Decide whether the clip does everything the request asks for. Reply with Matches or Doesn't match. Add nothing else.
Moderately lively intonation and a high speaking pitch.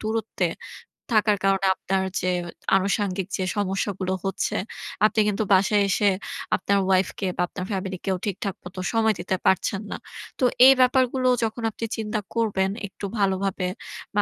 Doesn't match